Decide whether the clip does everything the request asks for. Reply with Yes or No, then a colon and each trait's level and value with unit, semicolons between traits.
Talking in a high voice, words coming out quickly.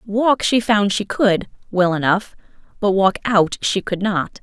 No: high, 200 Hz; average, 175 wpm